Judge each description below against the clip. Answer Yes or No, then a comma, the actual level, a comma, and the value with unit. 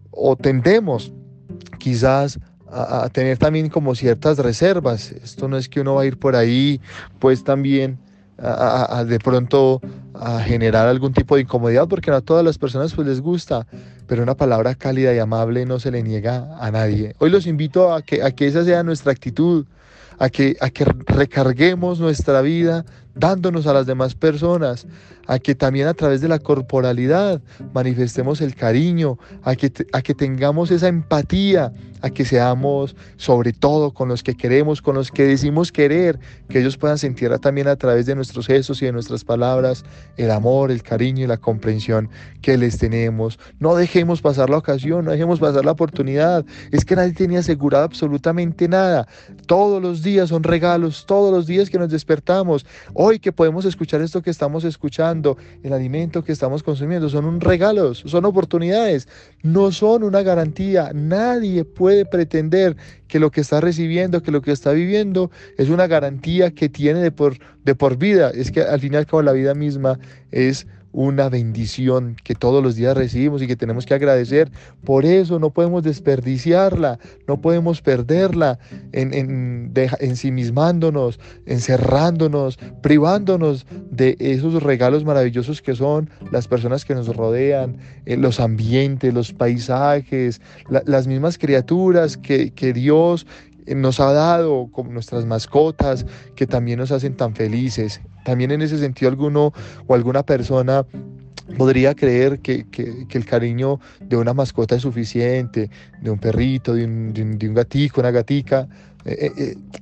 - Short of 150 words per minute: No, average, 170 wpm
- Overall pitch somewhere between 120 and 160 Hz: Yes, medium, 140 Hz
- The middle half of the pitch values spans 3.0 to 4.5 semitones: Yes, average, 4.1 semitones